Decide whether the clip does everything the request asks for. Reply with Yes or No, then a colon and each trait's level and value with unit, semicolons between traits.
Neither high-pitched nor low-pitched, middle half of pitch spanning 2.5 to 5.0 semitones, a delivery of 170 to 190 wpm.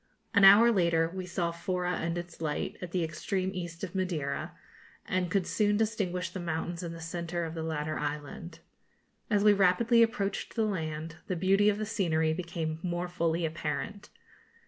Yes: medium, 175 Hz; average, 3.1 semitones; average, 175 wpm